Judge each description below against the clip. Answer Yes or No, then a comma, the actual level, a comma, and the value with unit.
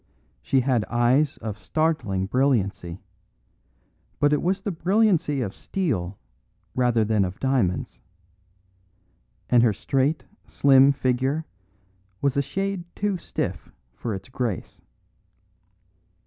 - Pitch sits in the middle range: No, low, 130 Hz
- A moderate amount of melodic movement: No, wide, 5.8 semitones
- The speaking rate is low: Yes, slow, 110 wpm